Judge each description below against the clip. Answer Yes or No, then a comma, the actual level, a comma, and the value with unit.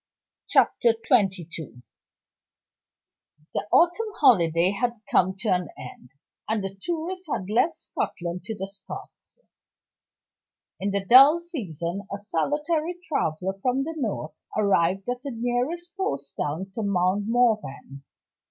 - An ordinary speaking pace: No, slow, 130 wpm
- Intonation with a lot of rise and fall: Yes, wide, 6.8 semitones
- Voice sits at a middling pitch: No, high, 205 Hz